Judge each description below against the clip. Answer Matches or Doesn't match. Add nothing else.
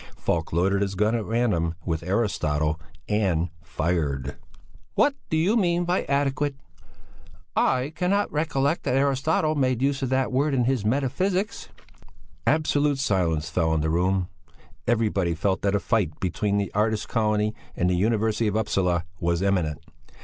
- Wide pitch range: Matches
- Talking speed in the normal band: Matches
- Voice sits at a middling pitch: Doesn't match